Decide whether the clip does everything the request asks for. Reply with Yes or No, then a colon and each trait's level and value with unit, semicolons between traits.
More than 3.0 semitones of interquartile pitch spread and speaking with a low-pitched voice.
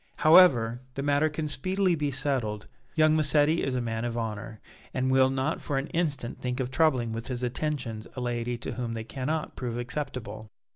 Yes: average, 4.0 semitones; low, 130 Hz